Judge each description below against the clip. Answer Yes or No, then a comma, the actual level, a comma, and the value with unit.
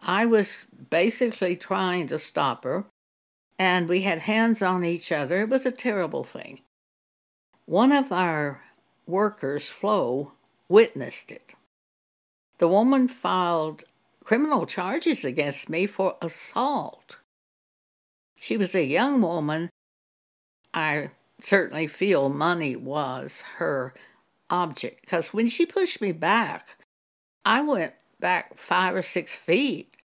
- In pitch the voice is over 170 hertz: Yes, medium, 185 Hz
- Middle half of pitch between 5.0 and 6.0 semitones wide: Yes, wide, 5.5 semitones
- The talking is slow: Yes, slow, 120 wpm